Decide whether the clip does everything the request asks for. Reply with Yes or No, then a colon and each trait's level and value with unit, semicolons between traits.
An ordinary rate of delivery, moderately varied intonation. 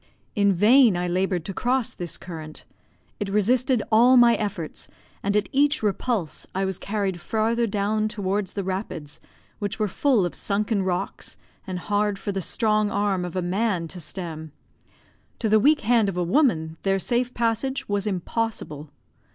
Yes: average, 165 wpm; average, 3.7 semitones